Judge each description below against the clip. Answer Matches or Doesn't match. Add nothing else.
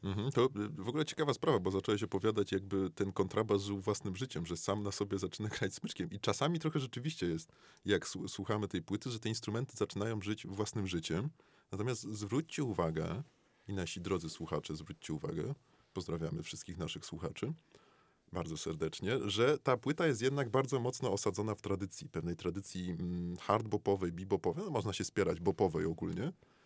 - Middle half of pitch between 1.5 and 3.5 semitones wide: Doesn't match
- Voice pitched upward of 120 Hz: Doesn't match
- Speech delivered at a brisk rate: Matches